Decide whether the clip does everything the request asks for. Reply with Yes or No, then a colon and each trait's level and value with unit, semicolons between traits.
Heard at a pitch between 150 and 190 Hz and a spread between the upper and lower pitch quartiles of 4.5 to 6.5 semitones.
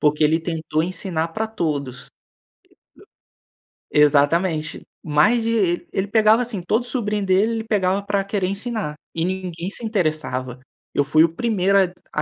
Yes: medium, 185 Hz; average, 5.3 semitones